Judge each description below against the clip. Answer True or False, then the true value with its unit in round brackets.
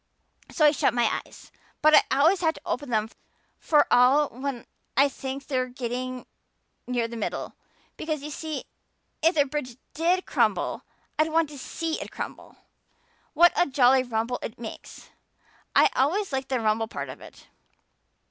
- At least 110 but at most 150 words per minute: False (165 wpm)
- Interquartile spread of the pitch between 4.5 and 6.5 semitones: False (3.8 semitones)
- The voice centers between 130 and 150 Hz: False (270 Hz)